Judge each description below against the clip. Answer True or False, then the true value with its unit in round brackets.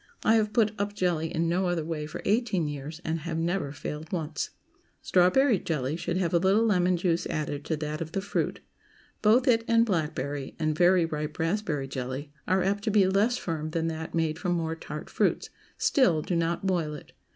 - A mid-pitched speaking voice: True (170 Hz)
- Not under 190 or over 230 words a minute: True (200 wpm)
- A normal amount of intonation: True (3.8 semitones)